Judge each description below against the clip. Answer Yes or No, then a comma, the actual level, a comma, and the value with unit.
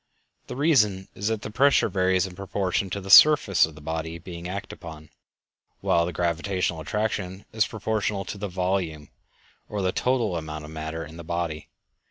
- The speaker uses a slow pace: No, average, 175 wpm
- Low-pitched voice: Yes, very low, 95 Hz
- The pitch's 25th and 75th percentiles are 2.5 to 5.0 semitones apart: Yes, average, 3.9 semitones